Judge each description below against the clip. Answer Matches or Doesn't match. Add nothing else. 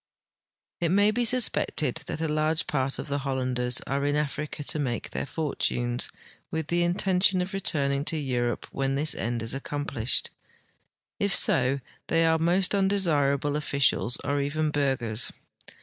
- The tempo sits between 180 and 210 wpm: Doesn't match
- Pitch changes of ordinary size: Matches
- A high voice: Doesn't match